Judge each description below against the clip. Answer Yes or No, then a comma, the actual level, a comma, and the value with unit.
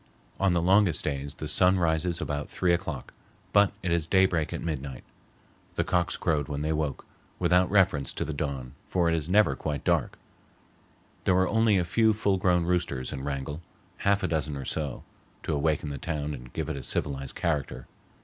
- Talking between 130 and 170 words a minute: No, average, 190 wpm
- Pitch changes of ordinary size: Yes, average, 4.1 semitones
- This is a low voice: Yes, very low, 80 Hz